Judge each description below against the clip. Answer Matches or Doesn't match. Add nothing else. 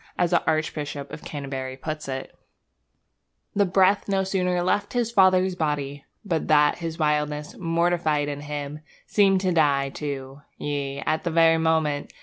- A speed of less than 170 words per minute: Matches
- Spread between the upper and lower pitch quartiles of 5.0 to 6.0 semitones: Doesn't match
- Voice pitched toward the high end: Doesn't match